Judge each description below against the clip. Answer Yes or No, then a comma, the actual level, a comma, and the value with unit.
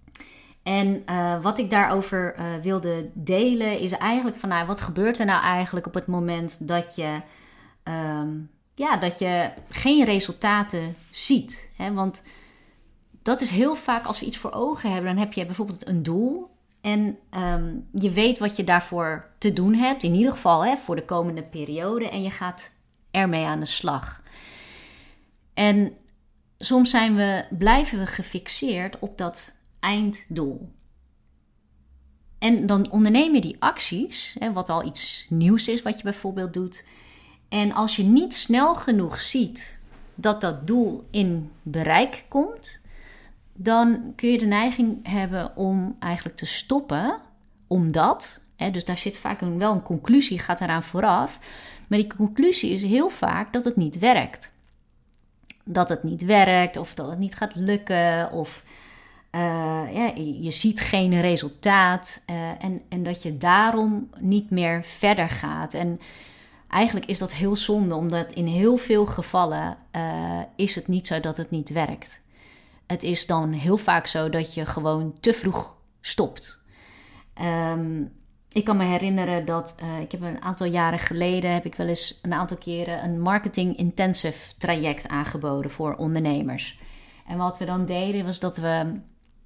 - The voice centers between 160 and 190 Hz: Yes, medium, 185 Hz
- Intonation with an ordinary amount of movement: Yes, average, 4.0 semitones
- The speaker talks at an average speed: Yes, average, 160 wpm